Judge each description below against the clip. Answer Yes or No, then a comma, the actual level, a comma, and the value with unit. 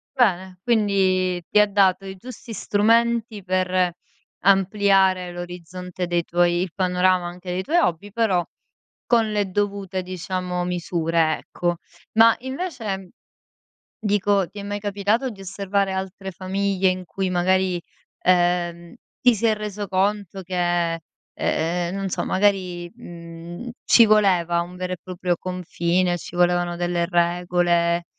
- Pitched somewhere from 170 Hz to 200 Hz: Yes, medium, 185 Hz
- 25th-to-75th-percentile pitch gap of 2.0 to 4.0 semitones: Yes, narrow, 2.4 semitones